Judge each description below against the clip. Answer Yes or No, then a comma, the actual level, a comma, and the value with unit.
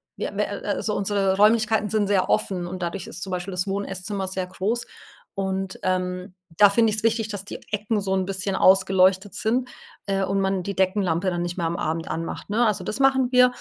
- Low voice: No, high, 195 Hz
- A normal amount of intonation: No, narrow, 2.2 semitones